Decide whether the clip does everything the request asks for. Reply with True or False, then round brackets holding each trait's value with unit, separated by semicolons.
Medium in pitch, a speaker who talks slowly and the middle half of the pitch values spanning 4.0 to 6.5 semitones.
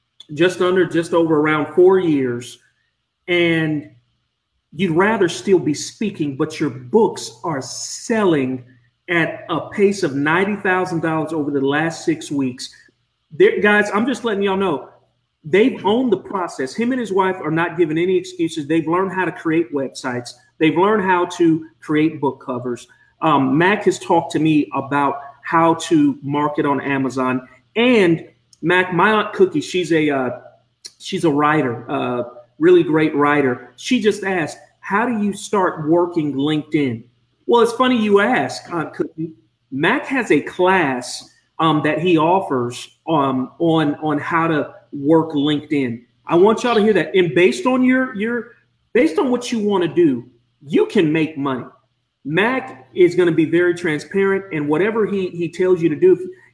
False (165 Hz; 170 wpm; 5.2 semitones)